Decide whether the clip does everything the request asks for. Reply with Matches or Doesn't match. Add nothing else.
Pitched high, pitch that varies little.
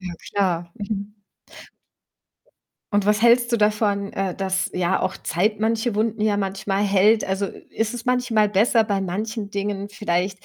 Matches